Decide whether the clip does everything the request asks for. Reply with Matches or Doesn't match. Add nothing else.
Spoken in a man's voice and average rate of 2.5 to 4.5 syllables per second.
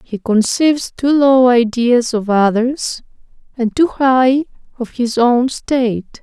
Doesn't match